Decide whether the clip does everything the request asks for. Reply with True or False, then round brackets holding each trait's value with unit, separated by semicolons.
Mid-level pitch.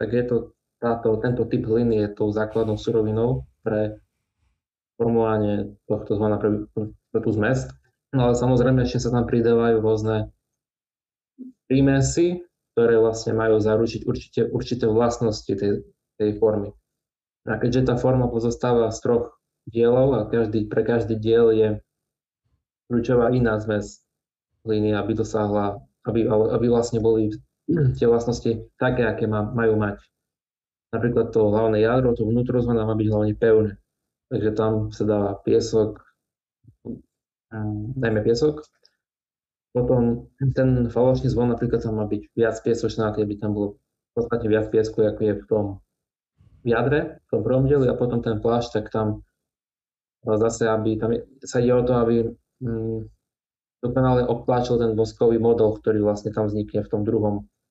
False (115 Hz)